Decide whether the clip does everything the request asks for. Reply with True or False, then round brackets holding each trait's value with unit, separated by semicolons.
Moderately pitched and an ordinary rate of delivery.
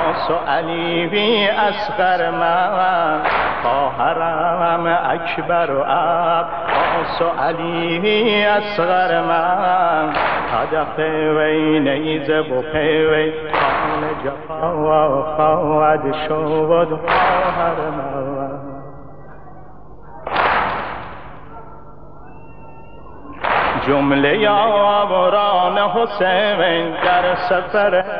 False (170 Hz; 90 wpm)